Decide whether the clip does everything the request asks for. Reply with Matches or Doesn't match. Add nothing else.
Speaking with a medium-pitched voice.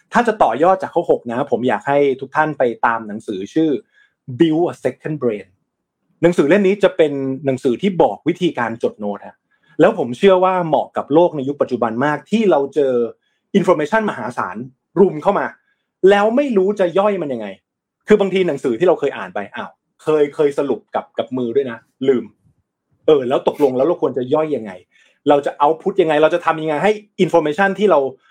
Matches